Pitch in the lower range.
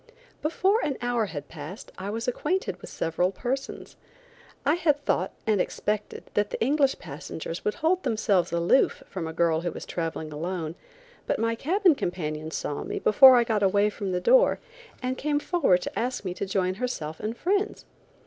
No: high, 210 Hz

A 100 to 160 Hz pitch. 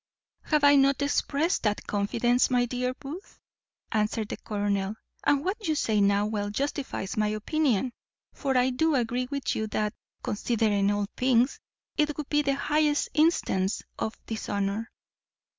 No: high, 245 Hz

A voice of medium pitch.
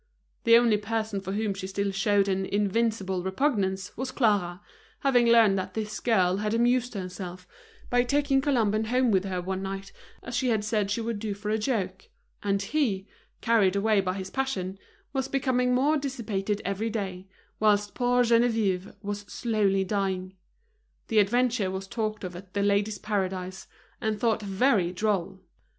No: high, 205 Hz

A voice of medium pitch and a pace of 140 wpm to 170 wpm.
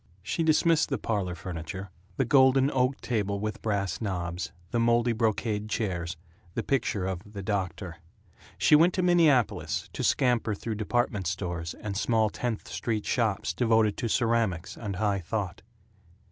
No: low, 110 Hz; average, 150 wpm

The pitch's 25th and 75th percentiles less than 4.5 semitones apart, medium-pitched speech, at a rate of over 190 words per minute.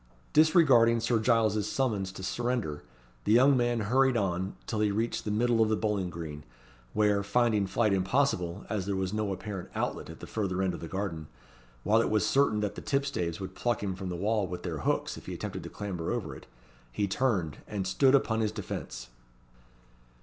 No: average, 3.8 semitones; low, 105 Hz; average, 200 wpm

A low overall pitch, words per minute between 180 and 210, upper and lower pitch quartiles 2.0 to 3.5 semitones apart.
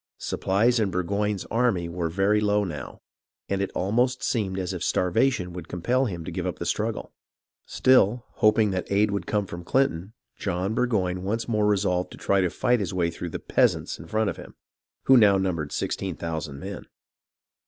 Yes: low, 100 Hz; average, 185 wpm; average, 3.2 semitones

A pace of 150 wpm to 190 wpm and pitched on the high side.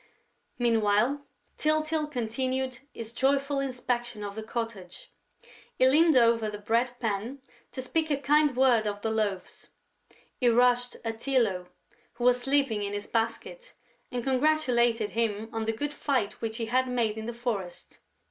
Yes: average, 155 wpm; high, 240 Hz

